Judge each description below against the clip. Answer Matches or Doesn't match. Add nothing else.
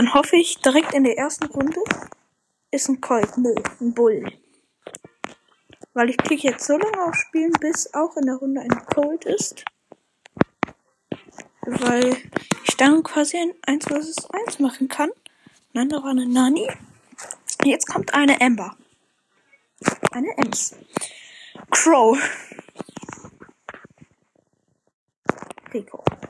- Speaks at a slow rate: Matches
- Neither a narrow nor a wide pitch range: Matches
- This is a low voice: Doesn't match